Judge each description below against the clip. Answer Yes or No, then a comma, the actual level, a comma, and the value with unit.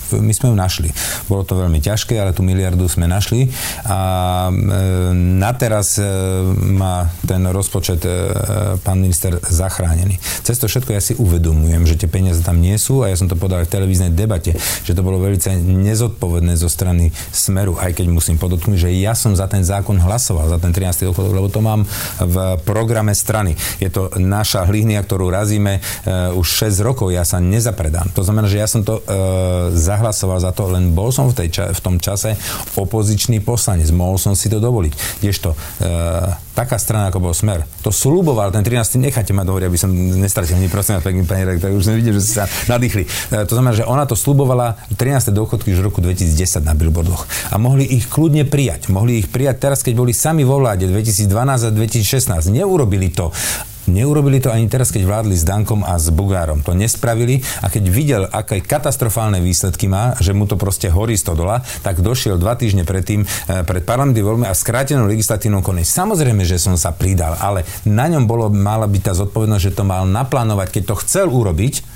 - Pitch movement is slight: No, average, 3.4 semitones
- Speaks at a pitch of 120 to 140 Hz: No, low, 100 Hz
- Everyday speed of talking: No, fast, 200 wpm